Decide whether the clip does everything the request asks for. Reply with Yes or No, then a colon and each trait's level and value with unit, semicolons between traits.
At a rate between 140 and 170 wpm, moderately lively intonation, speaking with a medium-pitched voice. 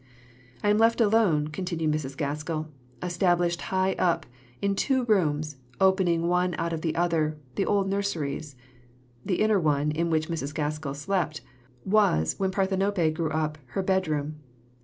Yes: average, 150 wpm; average, 3.9 semitones; medium, 170 Hz